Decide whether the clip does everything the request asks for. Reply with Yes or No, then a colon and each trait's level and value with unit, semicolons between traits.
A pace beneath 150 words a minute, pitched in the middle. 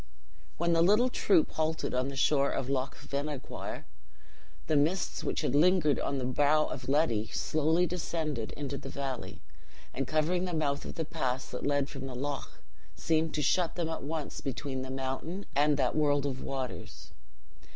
No: average, 175 wpm; medium, 145 Hz